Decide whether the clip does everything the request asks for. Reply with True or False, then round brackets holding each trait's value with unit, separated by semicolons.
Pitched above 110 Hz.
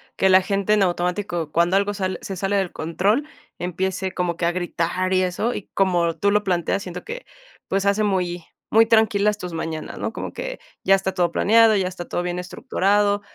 True (190 Hz)